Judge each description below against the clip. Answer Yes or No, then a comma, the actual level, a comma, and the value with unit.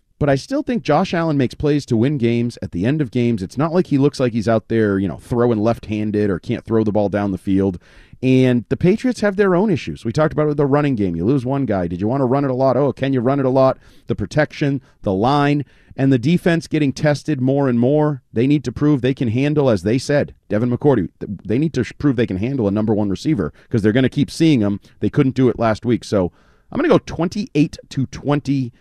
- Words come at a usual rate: No, fast, 265 wpm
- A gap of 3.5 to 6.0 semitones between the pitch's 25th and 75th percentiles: Yes, average, 4.6 semitones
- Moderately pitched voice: No, low, 130 Hz